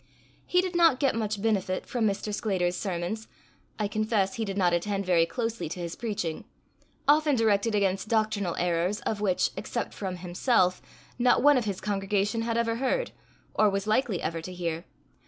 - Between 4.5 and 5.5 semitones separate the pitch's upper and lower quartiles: No, average, 3.8 semitones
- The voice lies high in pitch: Yes, high, 205 Hz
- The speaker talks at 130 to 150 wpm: No, average, 175 wpm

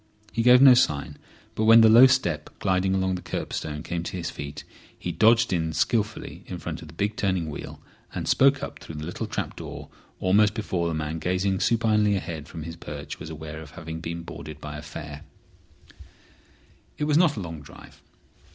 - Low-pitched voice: Yes, very low, 90 Hz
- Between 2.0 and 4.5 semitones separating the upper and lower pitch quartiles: No, wide, 5.6 semitones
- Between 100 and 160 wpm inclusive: No, average, 195 wpm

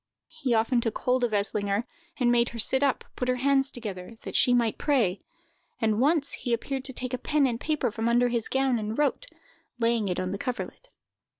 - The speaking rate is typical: No, fast, 210 wpm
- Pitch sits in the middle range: No, high, 245 Hz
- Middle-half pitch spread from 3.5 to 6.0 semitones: No, average, 3.0 semitones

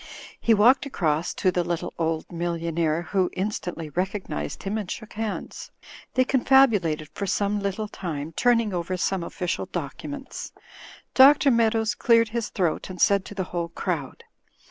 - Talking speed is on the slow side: No, average, 165 wpm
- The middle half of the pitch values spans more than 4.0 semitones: Yes, average, 4.7 semitones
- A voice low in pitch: No, high, 190 Hz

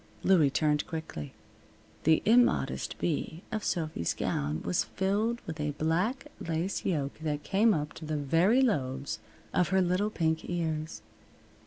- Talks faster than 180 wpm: No, average, 145 wpm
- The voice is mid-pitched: Yes, medium, 160 Hz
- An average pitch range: Yes, average, 4.2 semitones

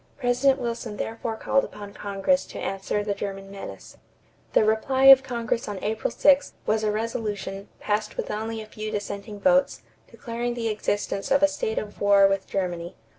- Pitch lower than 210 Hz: No, high, 215 Hz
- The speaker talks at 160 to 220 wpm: Yes, average, 175 wpm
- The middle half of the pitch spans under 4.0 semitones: Yes, average, 2.9 semitones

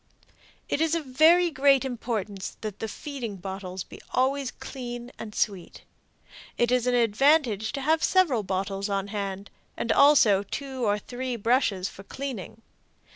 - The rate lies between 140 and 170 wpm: Yes, average, 150 wpm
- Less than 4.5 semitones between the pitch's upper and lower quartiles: No, average, 5.2 semitones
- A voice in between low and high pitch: No, high, 240 Hz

